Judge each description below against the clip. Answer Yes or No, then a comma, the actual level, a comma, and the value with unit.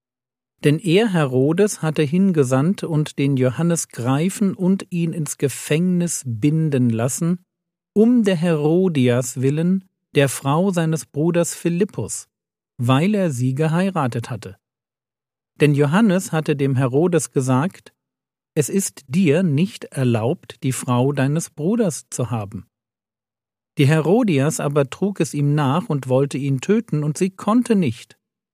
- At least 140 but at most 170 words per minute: No, average, 130 wpm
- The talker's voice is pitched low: No, medium, 150 Hz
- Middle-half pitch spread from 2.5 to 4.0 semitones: No, wide, 5.5 semitones